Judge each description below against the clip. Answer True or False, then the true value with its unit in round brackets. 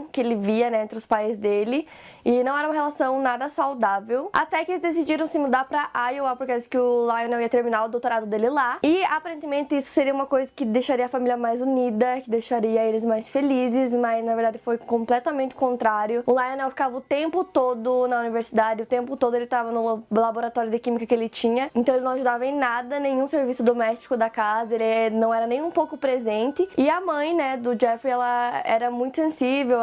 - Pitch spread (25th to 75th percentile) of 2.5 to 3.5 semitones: True (2.9 semitones)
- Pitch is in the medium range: False (245 Hz)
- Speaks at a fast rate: True (215 wpm)